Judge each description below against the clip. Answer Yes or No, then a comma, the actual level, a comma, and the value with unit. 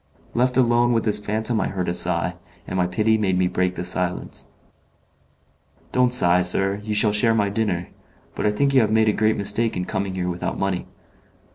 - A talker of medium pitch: No, low, 105 Hz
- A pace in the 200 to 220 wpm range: Yes, fast, 205 wpm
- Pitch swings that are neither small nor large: Yes, average, 3.5 semitones